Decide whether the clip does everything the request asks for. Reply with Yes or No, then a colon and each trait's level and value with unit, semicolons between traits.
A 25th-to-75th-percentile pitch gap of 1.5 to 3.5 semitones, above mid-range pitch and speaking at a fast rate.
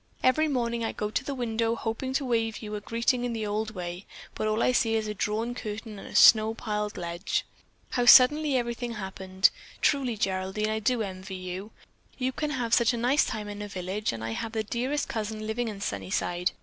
Yes: average, 2.8 semitones; high, 220 Hz; fast, 215 wpm